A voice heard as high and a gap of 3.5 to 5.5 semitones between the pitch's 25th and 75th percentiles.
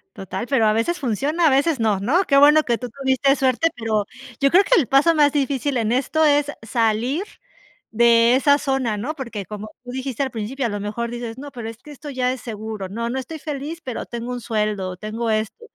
Yes: very high, 250 Hz; average, 4.1 semitones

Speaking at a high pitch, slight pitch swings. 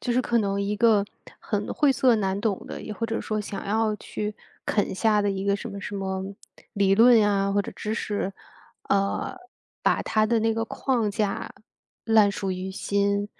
Yes: high, 205 Hz; narrow, 2.0 semitones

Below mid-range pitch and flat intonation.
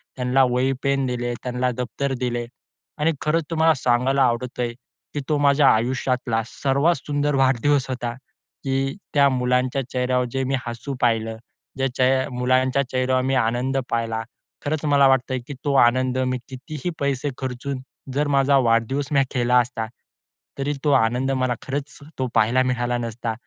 Yes: low, 130 Hz; narrow, 1.9 semitones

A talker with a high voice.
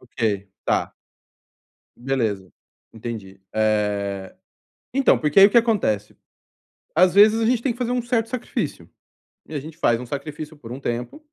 No: medium, 140 Hz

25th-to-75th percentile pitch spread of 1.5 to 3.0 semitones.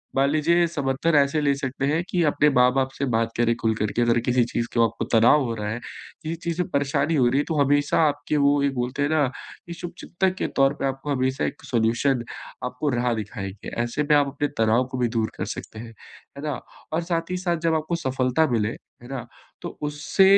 No: average, 3.9 semitones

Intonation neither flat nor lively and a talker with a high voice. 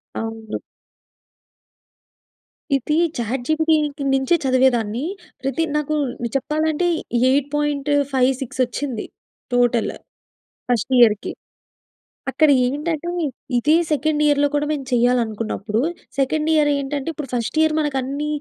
Yes: average, 3.5 semitones; very high, 275 Hz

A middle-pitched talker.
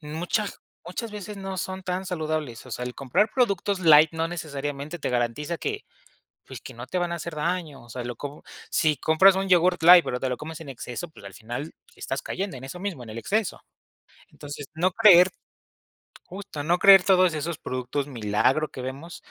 Yes: medium, 160 Hz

